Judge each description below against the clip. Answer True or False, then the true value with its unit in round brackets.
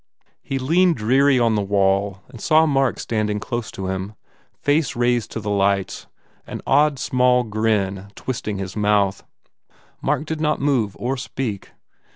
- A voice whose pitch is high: False (115 Hz)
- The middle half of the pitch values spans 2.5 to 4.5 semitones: False (5.0 semitones)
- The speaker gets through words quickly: False (160 wpm)